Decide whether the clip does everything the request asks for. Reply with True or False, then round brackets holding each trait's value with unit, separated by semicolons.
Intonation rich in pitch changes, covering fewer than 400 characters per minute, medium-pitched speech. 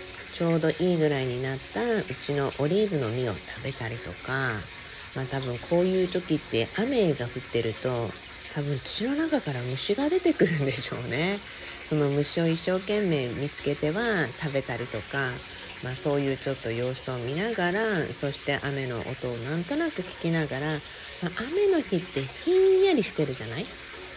True (6.3 semitones; 350 characters per minute; 145 Hz)